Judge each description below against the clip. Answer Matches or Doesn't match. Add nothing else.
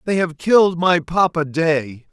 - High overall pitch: Doesn't match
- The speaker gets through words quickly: Doesn't match